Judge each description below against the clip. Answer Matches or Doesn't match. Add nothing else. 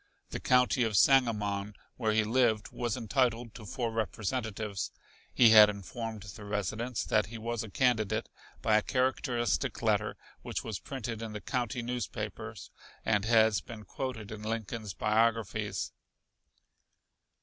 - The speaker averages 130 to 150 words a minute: Matches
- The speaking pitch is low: Matches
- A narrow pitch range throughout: Matches